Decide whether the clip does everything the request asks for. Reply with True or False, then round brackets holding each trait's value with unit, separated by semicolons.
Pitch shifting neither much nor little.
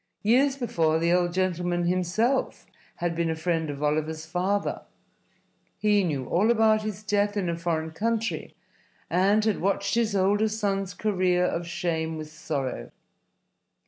True (4.0 semitones)